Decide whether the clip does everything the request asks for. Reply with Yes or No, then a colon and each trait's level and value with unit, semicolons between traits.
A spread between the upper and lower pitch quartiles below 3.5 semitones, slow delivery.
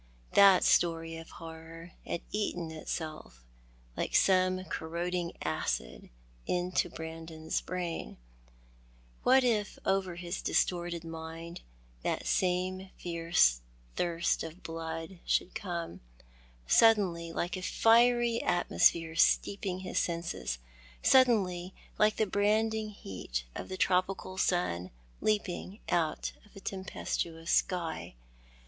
Yes: average, 2.7 semitones; slow, 115 wpm